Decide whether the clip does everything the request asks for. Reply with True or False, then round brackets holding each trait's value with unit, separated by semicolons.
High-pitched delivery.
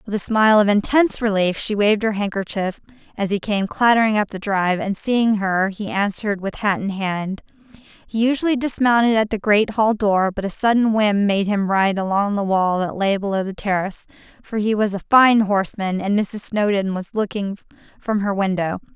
True (205 Hz)